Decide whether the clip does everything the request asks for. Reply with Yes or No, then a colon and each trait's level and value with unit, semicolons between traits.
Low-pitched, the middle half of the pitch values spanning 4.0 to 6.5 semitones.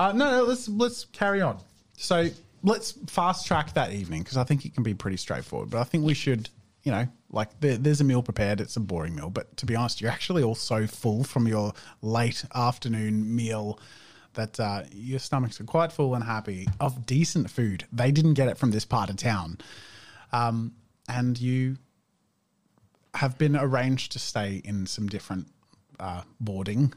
Yes: low, 120 Hz; average, 4.8 semitones